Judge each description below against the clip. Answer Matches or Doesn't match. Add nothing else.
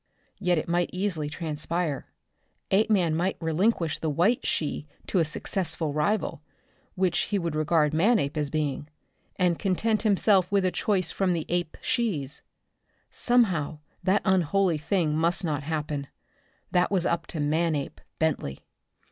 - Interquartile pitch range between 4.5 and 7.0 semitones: Doesn't match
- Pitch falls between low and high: Matches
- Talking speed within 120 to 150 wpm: Matches